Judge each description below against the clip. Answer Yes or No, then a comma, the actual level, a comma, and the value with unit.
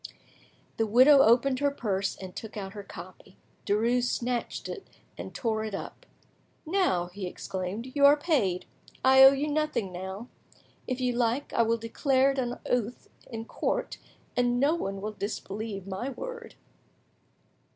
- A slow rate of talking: No, average, 155 wpm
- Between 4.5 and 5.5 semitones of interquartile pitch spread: Yes, average, 5.0 semitones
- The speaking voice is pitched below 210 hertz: No, high, 235 Hz